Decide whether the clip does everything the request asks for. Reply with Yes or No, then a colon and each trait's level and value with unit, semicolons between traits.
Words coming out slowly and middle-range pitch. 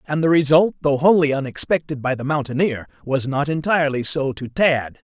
No: average, 175 wpm; medium, 145 Hz